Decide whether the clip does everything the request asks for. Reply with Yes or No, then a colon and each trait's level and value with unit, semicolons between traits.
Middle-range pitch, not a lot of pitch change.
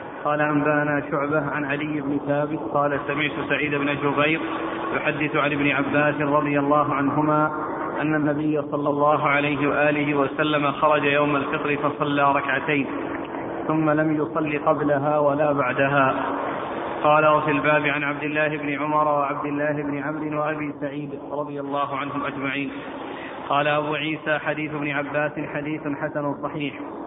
Yes: medium, 150 Hz; narrow, 0.9 semitones